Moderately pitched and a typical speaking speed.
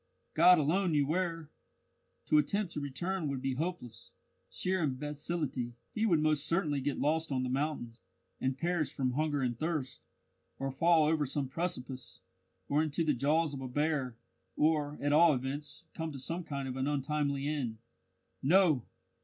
Yes: medium, 150 Hz; average, 165 wpm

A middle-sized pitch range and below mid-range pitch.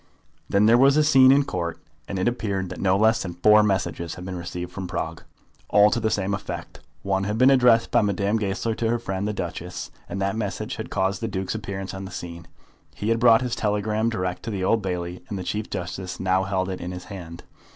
Yes: average, 3.1 semitones; low, 100 Hz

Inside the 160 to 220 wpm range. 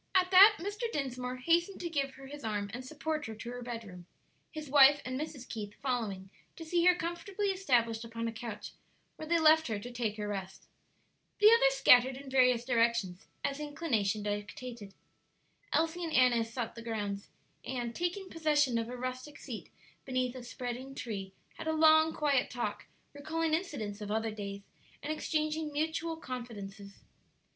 Yes: average, 170 wpm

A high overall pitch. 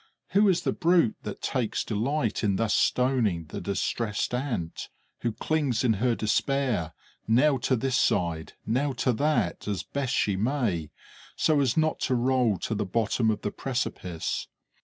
No: low, 120 Hz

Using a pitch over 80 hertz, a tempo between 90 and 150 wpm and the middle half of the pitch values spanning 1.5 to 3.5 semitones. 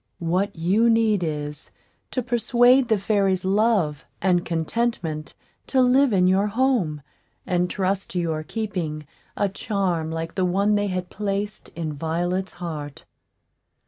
No: high, 190 Hz; average, 140 wpm; average, 4.5 semitones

